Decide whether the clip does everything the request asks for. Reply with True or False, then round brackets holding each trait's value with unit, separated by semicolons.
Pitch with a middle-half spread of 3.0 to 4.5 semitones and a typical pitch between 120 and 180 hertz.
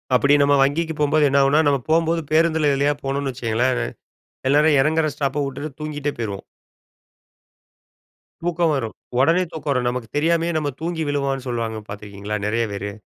True (3.7 semitones; 140 Hz)